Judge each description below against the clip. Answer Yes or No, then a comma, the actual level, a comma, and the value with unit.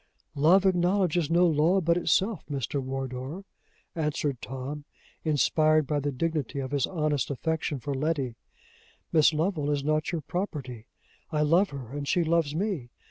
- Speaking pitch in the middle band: Yes, medium, 150 Hz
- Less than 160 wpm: Yes, average, 150 wpm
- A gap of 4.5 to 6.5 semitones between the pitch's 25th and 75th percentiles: No, average, 3.3 semitones